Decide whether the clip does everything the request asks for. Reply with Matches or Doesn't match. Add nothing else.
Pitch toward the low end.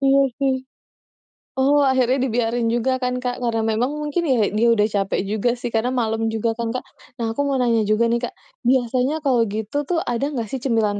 Doesn't match